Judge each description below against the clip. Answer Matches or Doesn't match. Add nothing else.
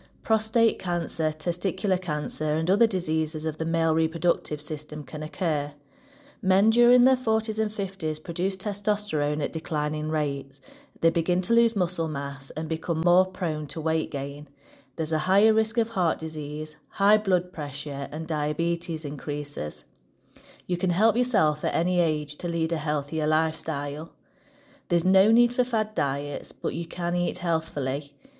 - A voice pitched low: Doesn't match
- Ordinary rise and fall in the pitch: Matches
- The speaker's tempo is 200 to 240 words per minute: Doesn't match